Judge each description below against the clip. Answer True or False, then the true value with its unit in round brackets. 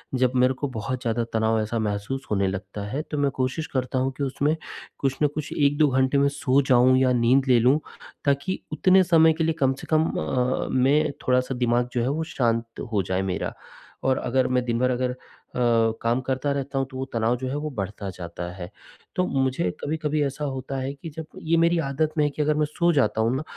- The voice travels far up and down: False (3.3 semitones)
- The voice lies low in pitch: True (130 Hz)